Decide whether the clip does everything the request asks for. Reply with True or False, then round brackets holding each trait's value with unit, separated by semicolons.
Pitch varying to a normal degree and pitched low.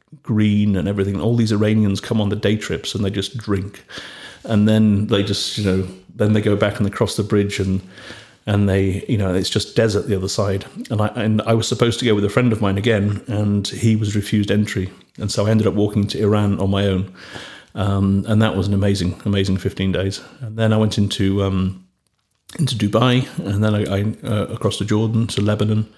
False (1.8 semitones; 105 Hz)